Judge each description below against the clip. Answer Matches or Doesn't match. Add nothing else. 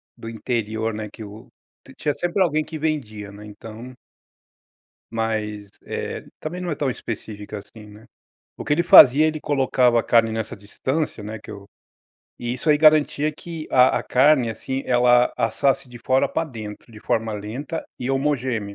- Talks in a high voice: Doesn't match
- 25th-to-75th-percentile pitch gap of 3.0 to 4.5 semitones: Doesn't match